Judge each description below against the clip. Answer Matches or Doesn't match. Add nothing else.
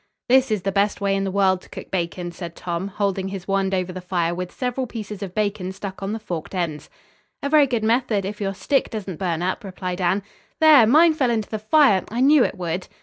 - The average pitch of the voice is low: Doesn't match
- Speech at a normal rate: Doesn't match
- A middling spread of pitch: Matches